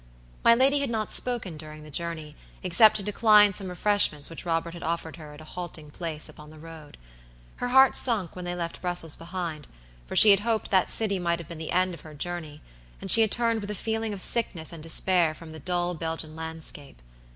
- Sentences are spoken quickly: Yes, fast, 220 wpm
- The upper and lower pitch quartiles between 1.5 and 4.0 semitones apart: No, average, 4.5 semitones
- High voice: No, medium, 175 Hz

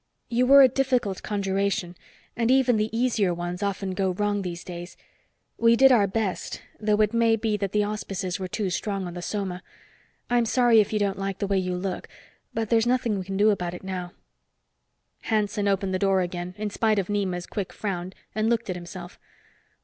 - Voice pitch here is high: Yes, high, 200 Hz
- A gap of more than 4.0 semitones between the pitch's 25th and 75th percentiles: No, average, 3.1 semitones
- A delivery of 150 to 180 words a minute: No, average, 200 wpm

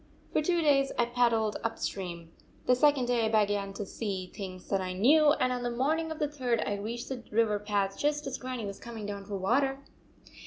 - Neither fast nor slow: No, fast, 225 wpm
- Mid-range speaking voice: No, high, 235 Hz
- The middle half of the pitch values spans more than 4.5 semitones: Yes, average, 5.0 semitones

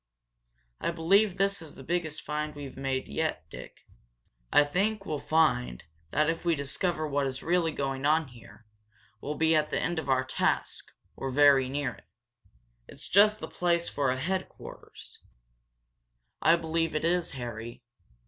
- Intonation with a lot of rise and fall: No, average, 4.1 semitones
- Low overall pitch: No, medium, 155 Hz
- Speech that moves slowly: No, average, 165 wpm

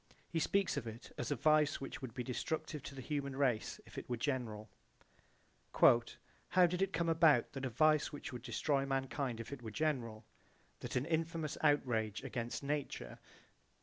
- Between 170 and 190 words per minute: Yes, average, 180 wpm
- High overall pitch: No, low, 135 Hz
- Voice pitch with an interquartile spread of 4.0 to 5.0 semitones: Yes, average, 4.3 semitones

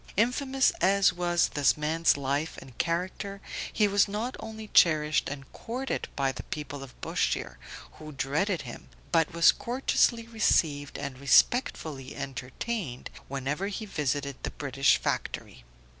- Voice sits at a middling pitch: Yes, medium, 155 Hz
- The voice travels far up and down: Yes, wide, 6.7 semitones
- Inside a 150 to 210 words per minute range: No, slow, 135 wpm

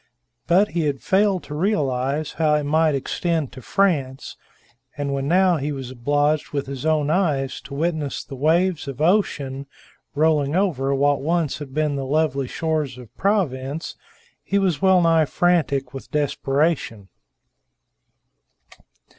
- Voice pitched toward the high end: No, medium, 150 Hz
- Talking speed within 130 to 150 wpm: Yes, average, 145 wpm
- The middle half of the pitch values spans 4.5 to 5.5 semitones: No, average, 3.5 semitones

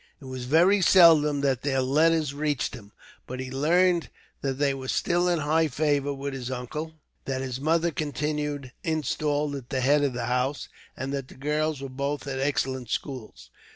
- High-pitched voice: No, medium, 140 Hz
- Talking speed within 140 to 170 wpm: No, average, 185 wpm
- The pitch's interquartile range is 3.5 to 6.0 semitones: No, average, 2.8 semitones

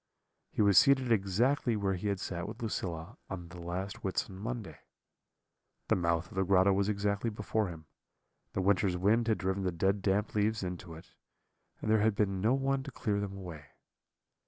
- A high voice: No, low, 100 Hz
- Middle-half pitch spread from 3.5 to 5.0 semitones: No, average, 3.0 semitones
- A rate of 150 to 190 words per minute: Yes, average, 185 wpm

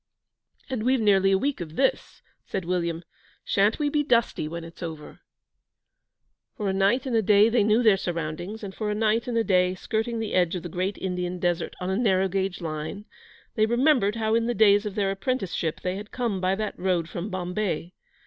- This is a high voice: Yes, high, 195 Hz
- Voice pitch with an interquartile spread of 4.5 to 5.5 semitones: No, average, 3.5 semitones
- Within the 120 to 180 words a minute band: No, fast, 205 wpm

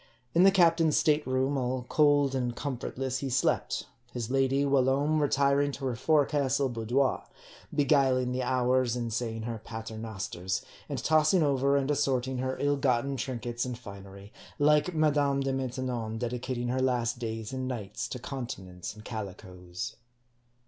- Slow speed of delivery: No, average, 150 wpm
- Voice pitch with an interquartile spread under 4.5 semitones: Yes, average, 2.9 semitones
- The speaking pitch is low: Yes, low, 130 Hz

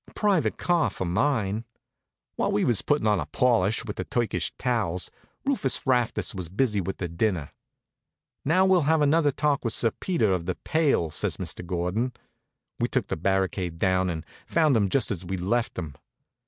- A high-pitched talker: No, low, 110 Hz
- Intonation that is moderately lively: No, wide, 7.1 semitones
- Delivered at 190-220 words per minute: No, average, 180 wpm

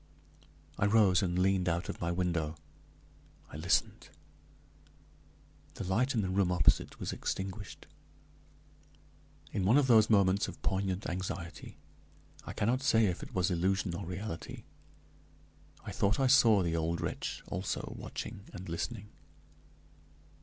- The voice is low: Yes, very low, 95 Hz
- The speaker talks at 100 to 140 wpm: Yes, slow, 135 wpm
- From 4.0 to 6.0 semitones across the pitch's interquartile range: No, average, 2.9 semitones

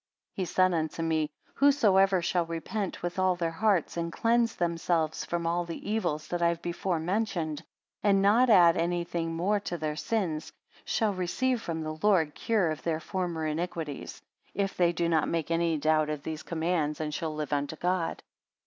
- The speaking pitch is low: No, medium, 170 Hz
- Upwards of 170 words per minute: Yes, average, 185 wpm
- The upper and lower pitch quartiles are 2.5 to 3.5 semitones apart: Yes, average, 2.9 semitones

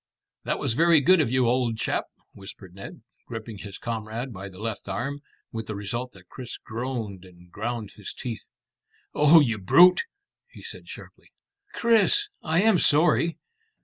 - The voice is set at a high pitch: No, low, 115 Hz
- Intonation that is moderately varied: No, wide, 6.2 semitones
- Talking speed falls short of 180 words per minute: Yes, average, 160 wpm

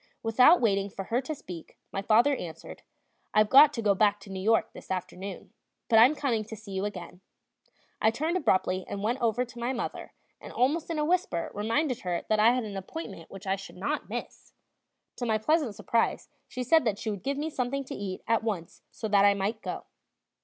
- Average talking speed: No, fast, 215 wpm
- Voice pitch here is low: No, high, 220 Hz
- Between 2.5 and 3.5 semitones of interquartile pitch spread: No, average, 4.5 semitones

